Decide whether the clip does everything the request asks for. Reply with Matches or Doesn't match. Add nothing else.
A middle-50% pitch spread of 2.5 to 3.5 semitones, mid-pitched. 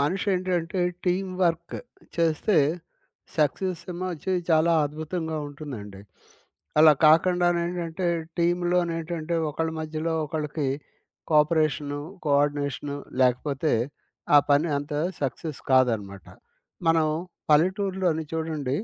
Matches